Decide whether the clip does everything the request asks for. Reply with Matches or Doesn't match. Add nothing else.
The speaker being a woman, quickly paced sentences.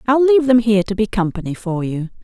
Matches